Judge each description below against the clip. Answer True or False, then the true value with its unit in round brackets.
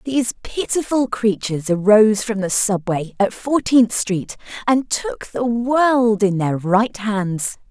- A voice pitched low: False (220 Hz)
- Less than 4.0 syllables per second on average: True (3.8 syllables/s)